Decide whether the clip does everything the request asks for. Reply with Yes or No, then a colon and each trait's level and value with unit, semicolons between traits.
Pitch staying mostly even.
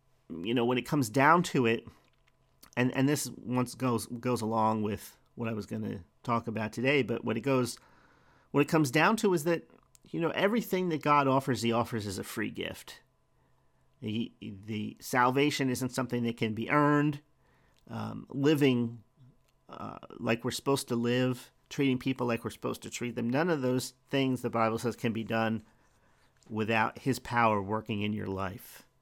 No: average, 3.1 semitones